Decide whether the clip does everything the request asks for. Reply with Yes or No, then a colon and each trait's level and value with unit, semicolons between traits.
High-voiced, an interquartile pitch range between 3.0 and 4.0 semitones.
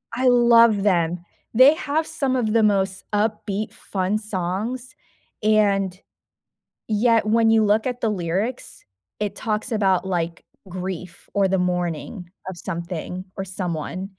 Yes: high, 205 Hz; average, 3.6 semitones